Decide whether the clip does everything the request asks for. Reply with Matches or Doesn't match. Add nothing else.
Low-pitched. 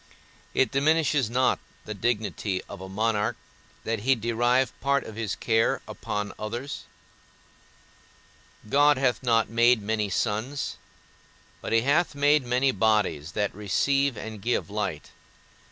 Matches